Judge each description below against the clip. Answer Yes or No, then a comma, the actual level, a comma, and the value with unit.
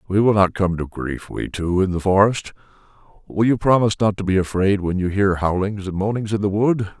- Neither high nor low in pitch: No, low, 100 Hz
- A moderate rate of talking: No, fast, 230 wpm